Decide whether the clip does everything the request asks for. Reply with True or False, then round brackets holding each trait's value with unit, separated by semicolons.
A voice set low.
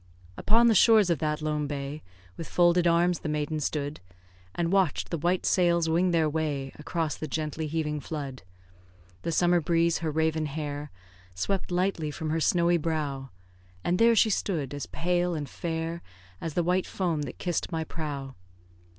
False (160 Hz)